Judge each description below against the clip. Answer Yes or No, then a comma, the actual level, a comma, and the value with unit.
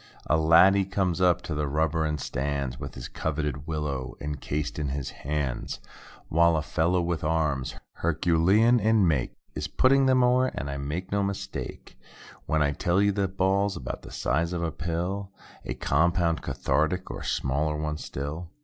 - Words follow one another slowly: No, average, 160 wpm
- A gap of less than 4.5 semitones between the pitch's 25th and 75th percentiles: Yes, average, 4.0 semitones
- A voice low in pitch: Yes, very low, 80 Hz